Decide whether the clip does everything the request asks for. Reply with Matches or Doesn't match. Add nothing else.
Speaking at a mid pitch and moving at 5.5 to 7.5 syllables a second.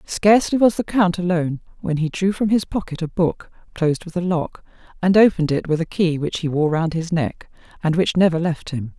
Matches